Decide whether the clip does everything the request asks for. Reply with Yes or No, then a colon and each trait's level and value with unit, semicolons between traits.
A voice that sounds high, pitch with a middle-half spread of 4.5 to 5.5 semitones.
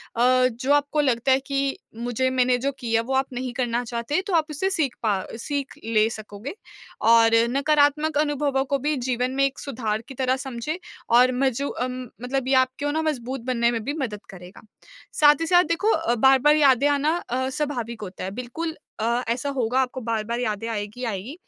No: very high, 260 Hz; average, 3.5 semitones